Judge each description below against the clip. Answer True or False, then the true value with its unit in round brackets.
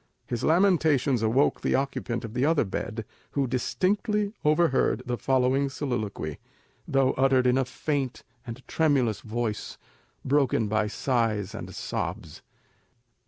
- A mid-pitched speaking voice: False (130 Hz)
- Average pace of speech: False (125 wpm)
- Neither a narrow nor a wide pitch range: True (3.7 semitones)